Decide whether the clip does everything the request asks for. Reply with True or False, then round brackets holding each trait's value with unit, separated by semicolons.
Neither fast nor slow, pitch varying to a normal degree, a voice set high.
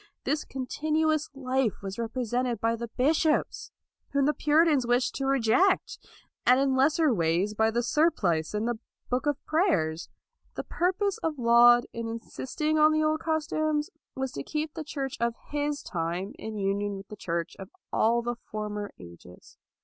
False (165 wpm; 6.1 semitones; 250 Hz)